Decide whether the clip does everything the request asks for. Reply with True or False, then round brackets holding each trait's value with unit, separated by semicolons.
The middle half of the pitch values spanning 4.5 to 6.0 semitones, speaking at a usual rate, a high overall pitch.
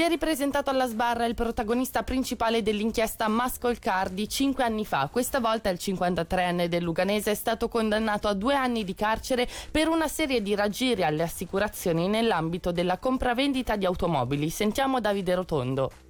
True (4.9 semitones; 155 wpm; 220 Hz)